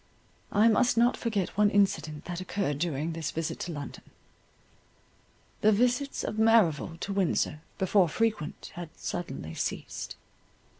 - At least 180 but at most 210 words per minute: No, slow, 135 wpm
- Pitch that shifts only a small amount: No, wide, 5.4 semitones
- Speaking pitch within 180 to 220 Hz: Yes, high, 190 Hz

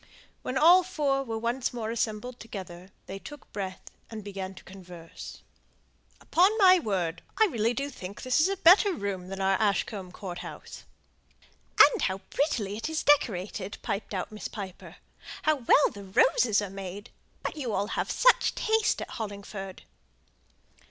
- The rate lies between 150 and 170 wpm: Yes, average, 160 wpm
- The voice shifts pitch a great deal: Yes, wide, 6.7 semitones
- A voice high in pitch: Yes, high, 215 Hz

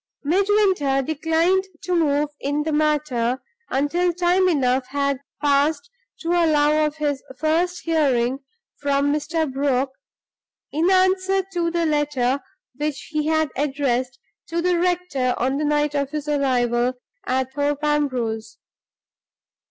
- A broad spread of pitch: No, average, 3.4 semitones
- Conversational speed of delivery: No, slow, 130 wpm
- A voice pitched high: Yes, very high, 295 Hz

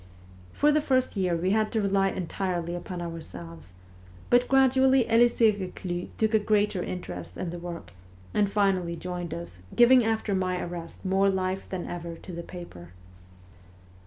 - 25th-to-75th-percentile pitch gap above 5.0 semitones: No, average, 4.0 semitones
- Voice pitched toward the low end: No, medium, 185 Hz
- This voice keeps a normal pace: Yes, average, 160 wpm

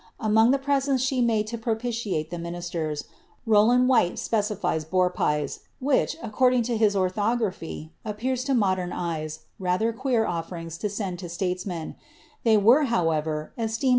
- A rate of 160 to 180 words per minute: No, average, 145 wpm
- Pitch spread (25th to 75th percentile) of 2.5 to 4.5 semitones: No, average, 5.3 semitones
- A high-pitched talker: Yes, high, 210 Hz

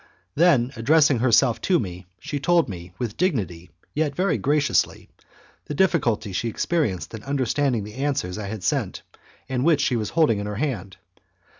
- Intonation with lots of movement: Yes, wide, 6.1 semitones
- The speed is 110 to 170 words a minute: Yes, average, 165 wpm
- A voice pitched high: No, low, 125 Hz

